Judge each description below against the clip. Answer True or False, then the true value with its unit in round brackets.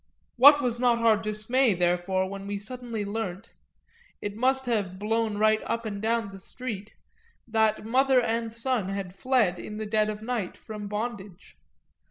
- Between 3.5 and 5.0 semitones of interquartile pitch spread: False (2.7 semitones)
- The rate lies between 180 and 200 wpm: False (165 wpm)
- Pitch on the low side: False (220 Hz)